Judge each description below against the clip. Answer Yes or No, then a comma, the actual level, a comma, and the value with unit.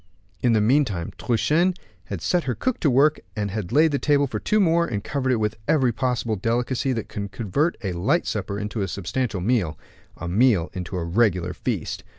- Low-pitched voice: Yes, low, 115 Hz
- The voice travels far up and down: Yes, wide, 5.8 semitones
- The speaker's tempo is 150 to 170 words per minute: No, average, 195 wpm